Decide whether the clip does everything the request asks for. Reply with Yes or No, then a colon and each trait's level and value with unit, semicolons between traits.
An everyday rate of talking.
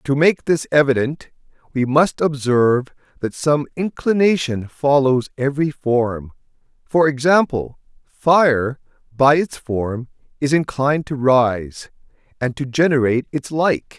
No: slow, 120 wpm